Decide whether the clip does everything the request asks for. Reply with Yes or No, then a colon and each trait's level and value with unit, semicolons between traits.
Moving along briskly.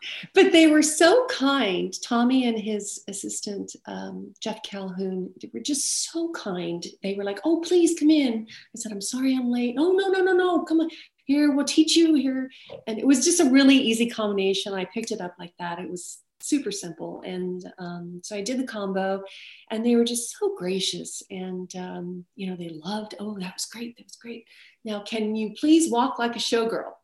Yes: fast, 210 wpm